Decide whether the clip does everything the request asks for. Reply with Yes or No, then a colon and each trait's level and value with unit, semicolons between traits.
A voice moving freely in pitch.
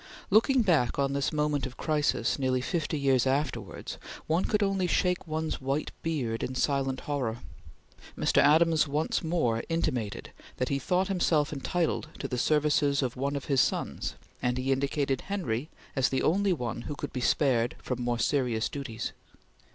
No: average, 3.7 semitones